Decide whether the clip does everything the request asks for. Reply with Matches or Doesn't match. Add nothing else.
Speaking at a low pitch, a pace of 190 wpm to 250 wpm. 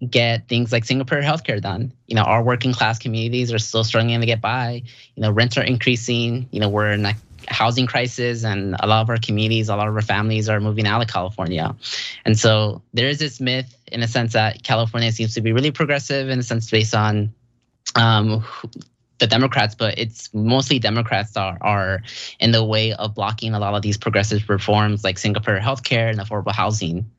Matches